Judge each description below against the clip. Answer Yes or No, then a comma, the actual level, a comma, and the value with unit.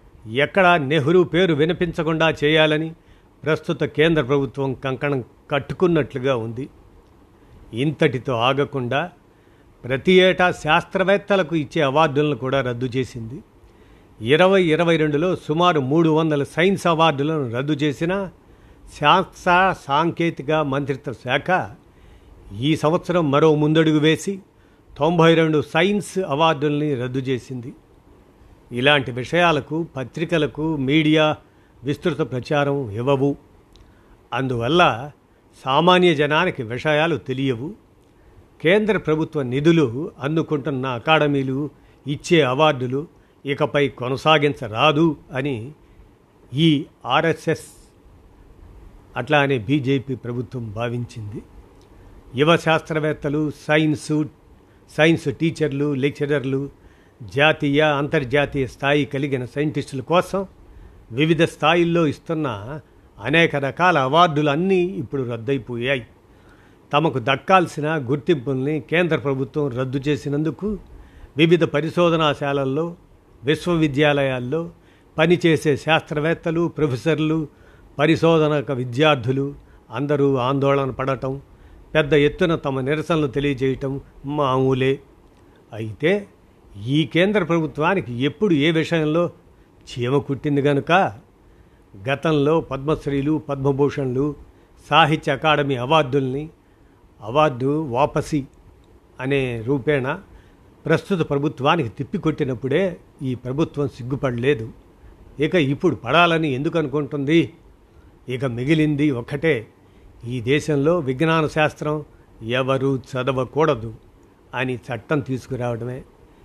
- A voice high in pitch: No, medium, 145 Hz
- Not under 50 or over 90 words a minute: Yes, average, 85 wpm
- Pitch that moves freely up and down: No, average, 3.4 semitones